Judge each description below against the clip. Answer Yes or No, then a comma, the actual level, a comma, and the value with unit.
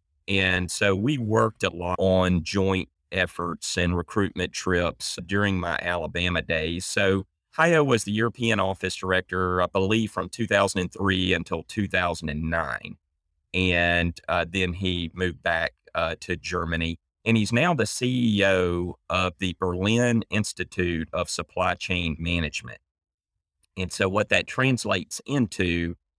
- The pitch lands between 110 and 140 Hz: No, very low, 90 Hz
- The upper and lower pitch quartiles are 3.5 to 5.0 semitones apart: No, narrow, 2.4 semitones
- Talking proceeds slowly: Yes, slow, 130 wpm